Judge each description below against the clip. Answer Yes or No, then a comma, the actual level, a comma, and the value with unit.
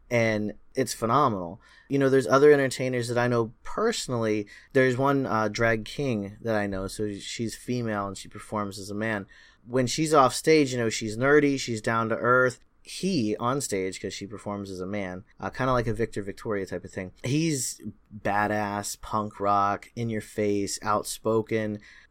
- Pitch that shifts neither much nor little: Yes, average, 3.7 semitones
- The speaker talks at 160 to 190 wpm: Yes, average, 185 wpm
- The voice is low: Yes, low, 110 Hz